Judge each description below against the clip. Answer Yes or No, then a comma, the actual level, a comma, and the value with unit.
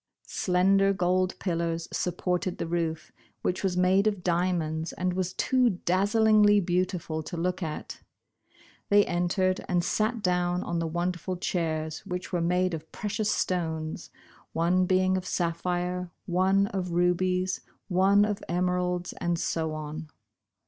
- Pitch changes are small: Yes, narrow, 1.5 semitones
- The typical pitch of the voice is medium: Yes, medium, 180 Hz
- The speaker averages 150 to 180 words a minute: No, average, 140 wpm